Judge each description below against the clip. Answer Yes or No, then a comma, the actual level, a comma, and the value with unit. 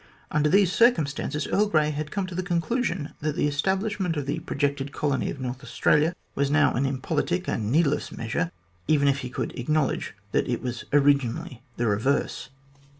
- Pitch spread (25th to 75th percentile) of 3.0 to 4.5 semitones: Yes, average, 3.7 semitones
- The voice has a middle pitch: Yes, medium, 145 Hz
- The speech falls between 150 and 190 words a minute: Yes, average, 175 wpm